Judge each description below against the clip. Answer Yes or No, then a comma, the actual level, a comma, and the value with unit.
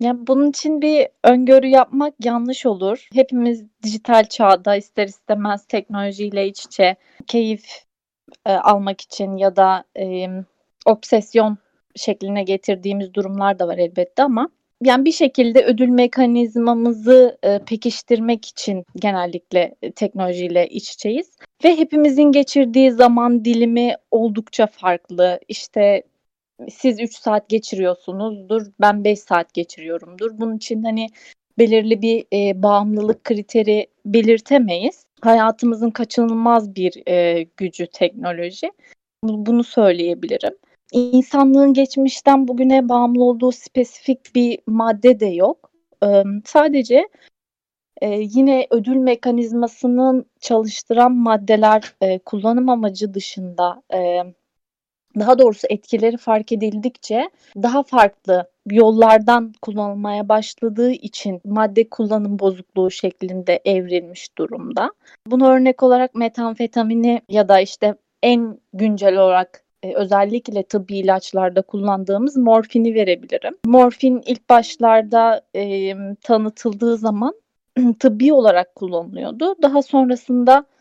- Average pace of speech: Yes, average, 110 wpm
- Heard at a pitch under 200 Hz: No, high, 225 Hz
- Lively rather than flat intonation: No, average, 3.8 semitones